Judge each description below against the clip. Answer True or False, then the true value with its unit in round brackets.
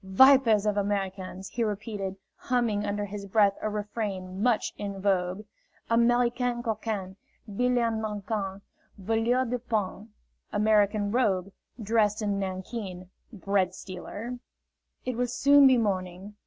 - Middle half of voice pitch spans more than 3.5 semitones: False (3.1 semitones)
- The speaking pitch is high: True (210 Hz)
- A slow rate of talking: True (125 wpm)